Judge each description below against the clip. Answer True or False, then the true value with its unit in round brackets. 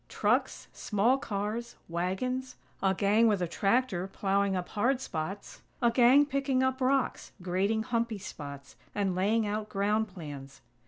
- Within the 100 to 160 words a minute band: True (145 wpm)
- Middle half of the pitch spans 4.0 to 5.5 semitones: True (4.5 semitones)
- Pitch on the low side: False (210 Hz)